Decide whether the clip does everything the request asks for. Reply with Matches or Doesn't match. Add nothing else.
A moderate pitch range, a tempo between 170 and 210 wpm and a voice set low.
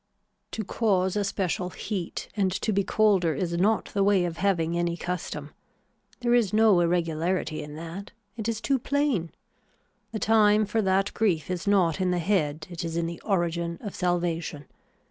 Doesn't match